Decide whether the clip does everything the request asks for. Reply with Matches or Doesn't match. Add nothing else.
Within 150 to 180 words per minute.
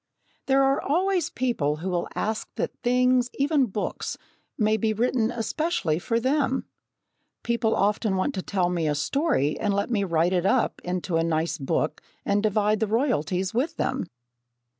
Matches